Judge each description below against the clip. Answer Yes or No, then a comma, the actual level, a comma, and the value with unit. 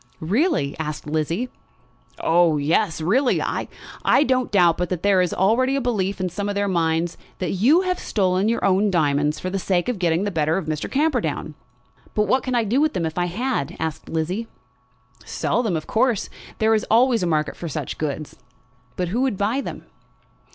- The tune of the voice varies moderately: No, wide, 6.2 semitones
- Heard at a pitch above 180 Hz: Yes, high, 190 Hz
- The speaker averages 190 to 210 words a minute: Yes, average, 195 wpm